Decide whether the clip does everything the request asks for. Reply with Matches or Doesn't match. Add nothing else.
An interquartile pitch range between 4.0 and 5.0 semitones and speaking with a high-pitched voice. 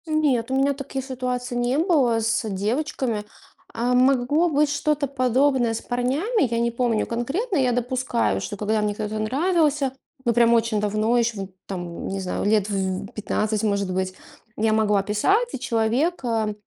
Matches